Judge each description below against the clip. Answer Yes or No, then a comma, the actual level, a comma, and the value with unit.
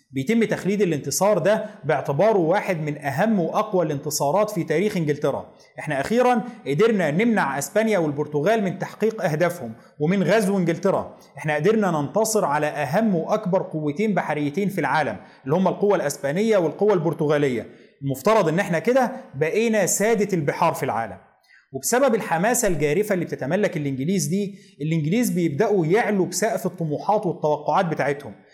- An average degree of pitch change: No, wide, 5.8 semitones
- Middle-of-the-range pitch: Yes, medium, 180 Hz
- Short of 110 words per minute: No, fast, 135 wpm